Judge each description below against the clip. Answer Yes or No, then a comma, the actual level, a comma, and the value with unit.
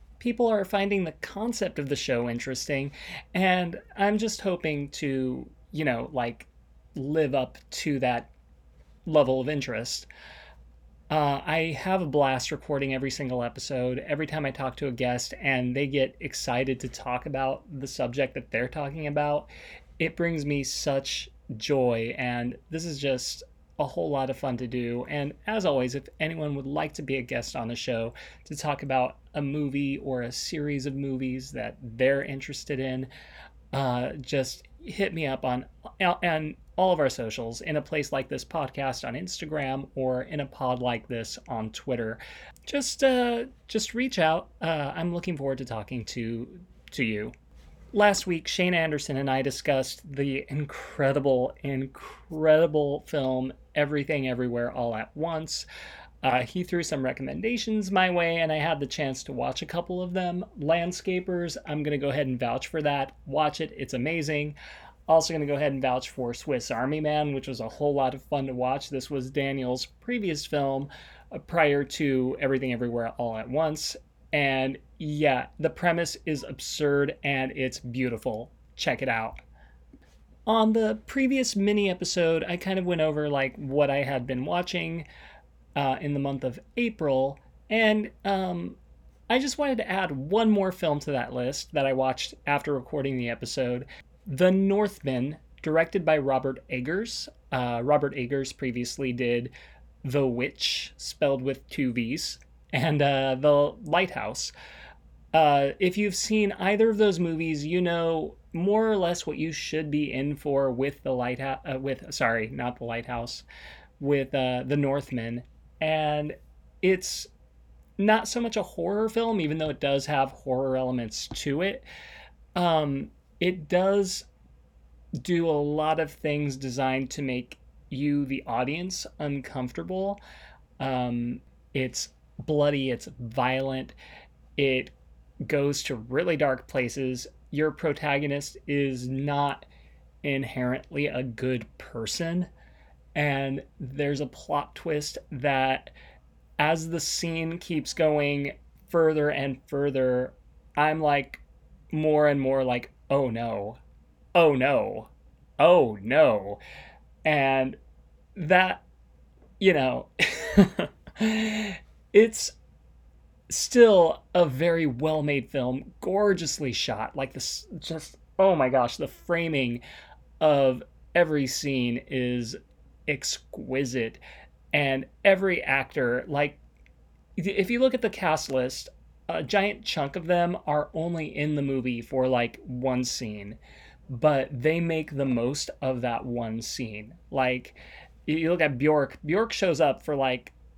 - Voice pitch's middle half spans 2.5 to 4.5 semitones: Yes, average, 4.2 semitones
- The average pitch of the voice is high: No, medium, 140 Hz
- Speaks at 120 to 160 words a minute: Yes, average, 150 wpm